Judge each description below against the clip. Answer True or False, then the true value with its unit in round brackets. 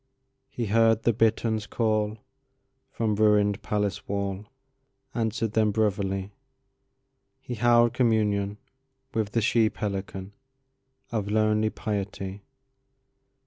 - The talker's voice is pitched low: True (110 Hz)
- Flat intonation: True (1.9 semitones)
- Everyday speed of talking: False (75 wpm)